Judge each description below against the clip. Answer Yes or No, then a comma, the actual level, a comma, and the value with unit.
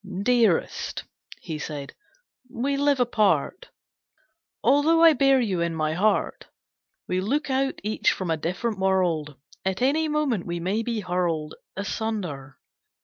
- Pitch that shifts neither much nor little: No, wide, 7.7 semitones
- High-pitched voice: Yes, high, 205 Hz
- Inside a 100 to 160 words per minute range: Yes, slow, 135 wpm